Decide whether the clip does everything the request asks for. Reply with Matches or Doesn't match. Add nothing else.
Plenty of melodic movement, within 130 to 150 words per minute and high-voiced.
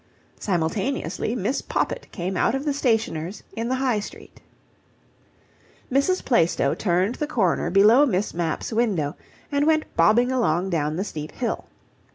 Matches